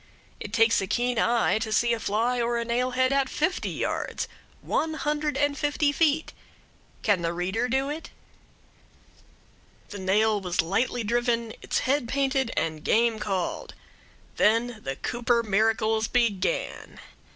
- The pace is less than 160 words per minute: Yes, average, 140 wpm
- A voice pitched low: No, high, 235 Hz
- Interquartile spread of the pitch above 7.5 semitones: No, average, 3.5 semitones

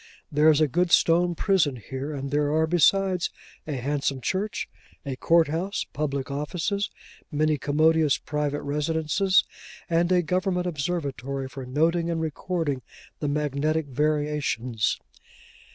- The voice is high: No, medium, 150 Hz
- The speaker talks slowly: Yes, slow, 130 wpm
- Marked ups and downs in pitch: No, average, 3.2 semitones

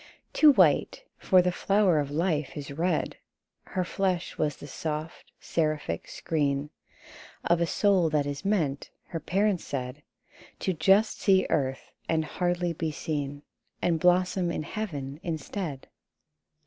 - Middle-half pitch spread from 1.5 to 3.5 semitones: No, average, 3.9 semitones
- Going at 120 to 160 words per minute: Yes, slow, 135 wpm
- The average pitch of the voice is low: No, medium, 165 Hz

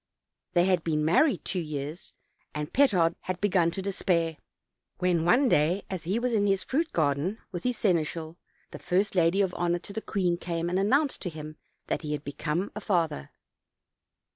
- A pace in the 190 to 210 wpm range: Yes, fast, 205 wpm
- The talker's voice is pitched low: No, medium, 175 Hz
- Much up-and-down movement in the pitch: No, average, 3.5 semitones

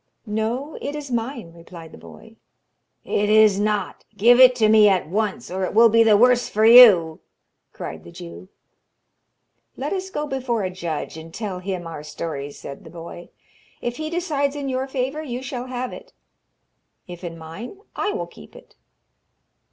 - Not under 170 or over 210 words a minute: Yes, average, 175 wpm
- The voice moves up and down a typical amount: No, wide, 6.3 semitones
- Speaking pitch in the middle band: No, high, 220 Hz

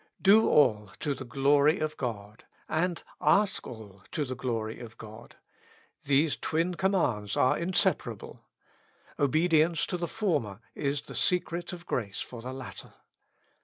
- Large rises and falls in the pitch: Yes, wide, 6.6 semitones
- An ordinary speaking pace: Yes, average, 150 wpm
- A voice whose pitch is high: No, medium, 140 Hz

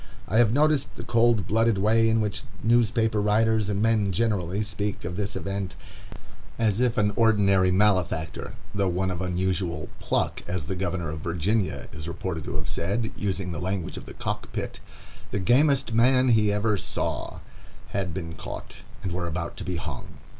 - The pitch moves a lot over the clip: No, average, 3.8 semitones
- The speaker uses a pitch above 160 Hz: No, low, 100 Hz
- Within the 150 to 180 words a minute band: Yes, average, 170 wpm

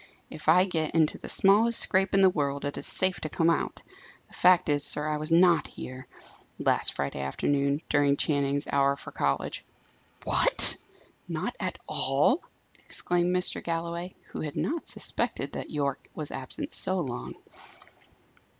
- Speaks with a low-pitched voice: No, medium, 155 Hz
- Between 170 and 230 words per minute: No, average, 160 wpm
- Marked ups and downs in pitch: No, average, 4.2 semitones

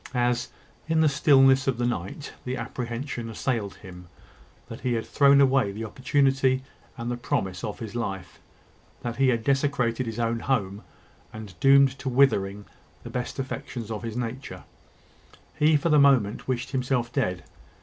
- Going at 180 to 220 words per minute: No, average, 160 wpm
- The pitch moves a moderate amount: Yes, average, 3.2 semitones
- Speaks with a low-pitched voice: Yes, low, 125 Hz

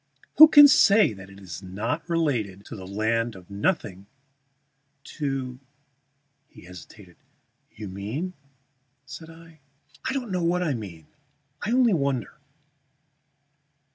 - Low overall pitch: Yes, low, 130 Hz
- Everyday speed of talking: No, slow, 130 wpm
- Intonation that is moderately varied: No, wide, 8.9 semitones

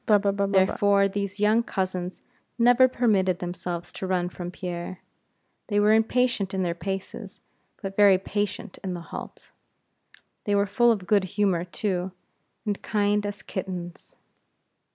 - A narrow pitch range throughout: Yes, narrow, 2.1 semitones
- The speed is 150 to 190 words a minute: No, slow, 135 wpm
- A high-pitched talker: Yes, high, 195 Hz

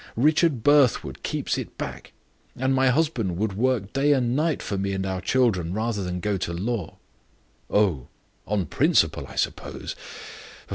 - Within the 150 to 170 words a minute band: Yes, average, 155 wpm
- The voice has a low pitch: Yes, low, 110 Hz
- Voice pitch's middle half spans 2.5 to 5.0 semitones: No, wide, 5.6 semitones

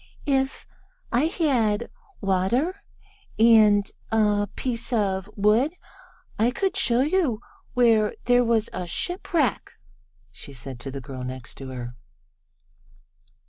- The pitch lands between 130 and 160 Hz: No, high, 220 Hz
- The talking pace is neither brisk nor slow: No, slow, 115 wpm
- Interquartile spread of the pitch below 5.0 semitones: No, wide, 5.5 semitones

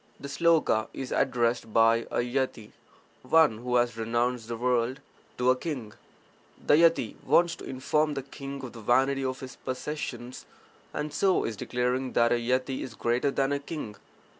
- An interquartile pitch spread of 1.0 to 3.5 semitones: Yes, average, 2.8 semitones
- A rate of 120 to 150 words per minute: No, average, 170 wpm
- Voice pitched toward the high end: No, low, 130 Hz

